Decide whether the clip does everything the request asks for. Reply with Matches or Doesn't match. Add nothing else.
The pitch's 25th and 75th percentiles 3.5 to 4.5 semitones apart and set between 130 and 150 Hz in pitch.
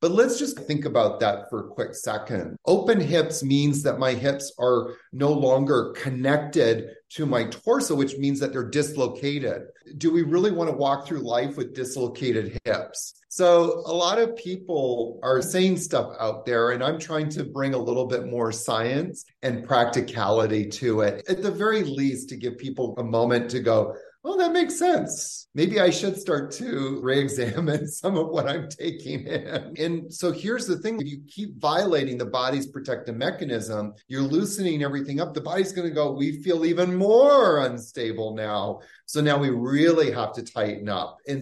Doesn't match